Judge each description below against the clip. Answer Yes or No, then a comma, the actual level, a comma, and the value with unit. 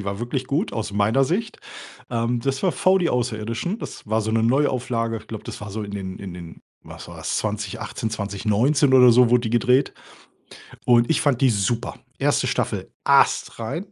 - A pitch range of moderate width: Yes, average, 3.5 semitones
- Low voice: Yes, low, 115 Hz